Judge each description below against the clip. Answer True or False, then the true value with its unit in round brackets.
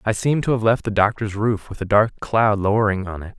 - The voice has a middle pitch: False (105 Hz)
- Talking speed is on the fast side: True (265 wpm)